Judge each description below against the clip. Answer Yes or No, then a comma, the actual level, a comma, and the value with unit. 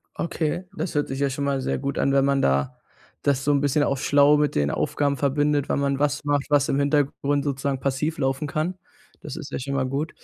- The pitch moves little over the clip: Yes, narrow, 1.3 semitones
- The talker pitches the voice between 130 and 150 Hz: Yes, medium, 140 Hz